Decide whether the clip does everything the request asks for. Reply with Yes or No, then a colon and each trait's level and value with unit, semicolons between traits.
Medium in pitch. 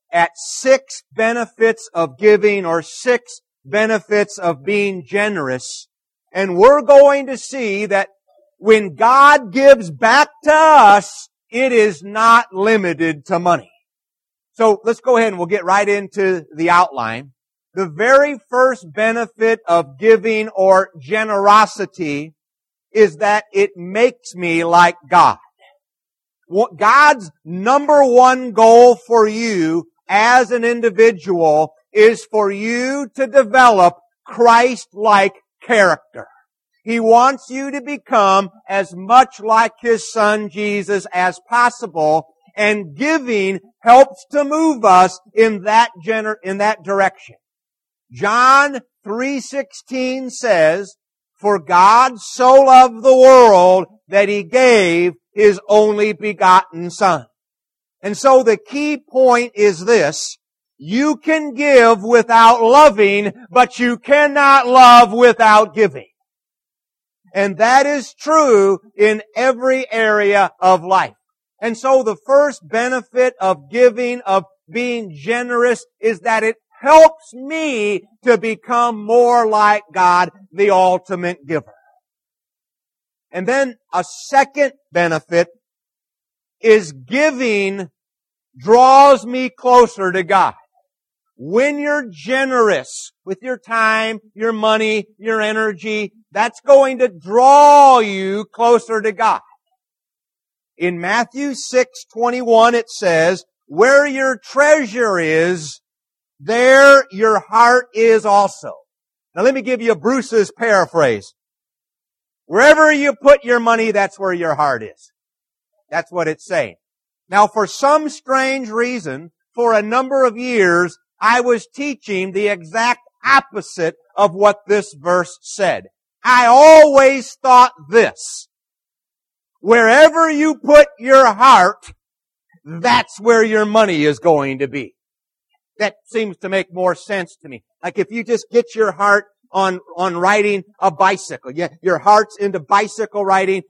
No: high, 220 Hz